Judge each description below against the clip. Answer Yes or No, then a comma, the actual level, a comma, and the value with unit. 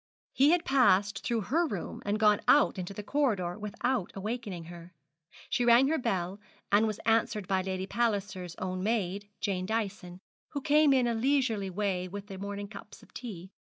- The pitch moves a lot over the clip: No, average, 4.1 semitones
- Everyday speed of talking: Yes, average, 180 wpm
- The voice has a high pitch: Yes, high, 205 Hz